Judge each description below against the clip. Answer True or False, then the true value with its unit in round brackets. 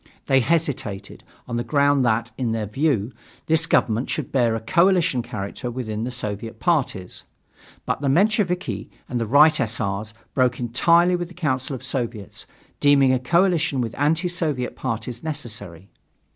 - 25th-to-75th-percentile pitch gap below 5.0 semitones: False (5.6 semitones)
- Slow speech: False (160 wpm)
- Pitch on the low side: True (130 Hz)